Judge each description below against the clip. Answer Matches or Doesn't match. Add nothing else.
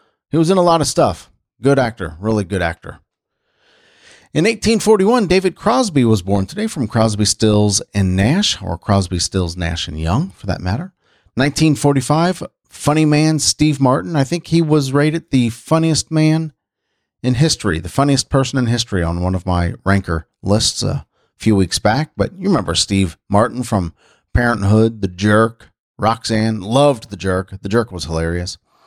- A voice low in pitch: Matches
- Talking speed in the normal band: Matches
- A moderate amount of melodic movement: Doesn't match